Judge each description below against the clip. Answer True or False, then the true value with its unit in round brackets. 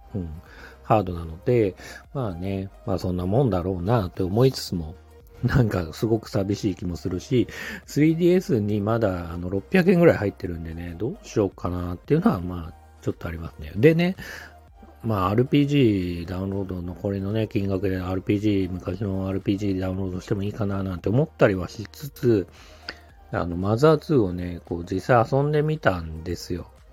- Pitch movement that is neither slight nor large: True (4.4 semitones)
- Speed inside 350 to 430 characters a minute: True (355 characters per minute)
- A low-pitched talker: True (95 Hz)